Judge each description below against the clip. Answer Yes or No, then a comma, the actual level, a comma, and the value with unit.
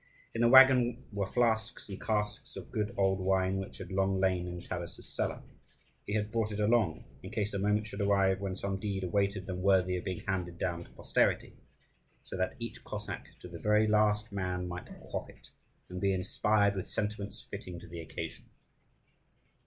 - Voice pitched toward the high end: No, low, 100 Hz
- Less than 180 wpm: No, average, 190 wpm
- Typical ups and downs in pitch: No, narrow, 2.3 semitones